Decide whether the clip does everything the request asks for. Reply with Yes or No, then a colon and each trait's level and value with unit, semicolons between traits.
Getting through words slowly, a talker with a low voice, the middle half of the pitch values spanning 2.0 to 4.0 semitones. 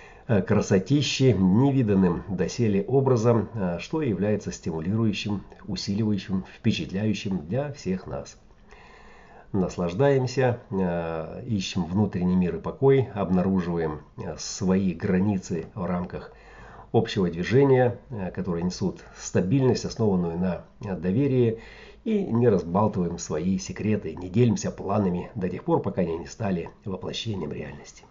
No: slow, 105 wpm; low, 100 Hz; average, 4.8 semitones